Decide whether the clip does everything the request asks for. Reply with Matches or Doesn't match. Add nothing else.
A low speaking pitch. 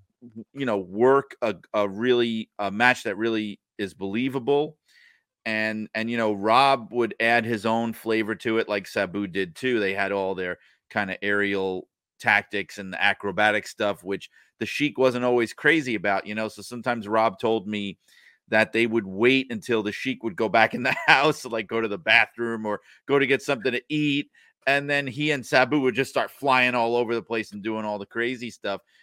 Matches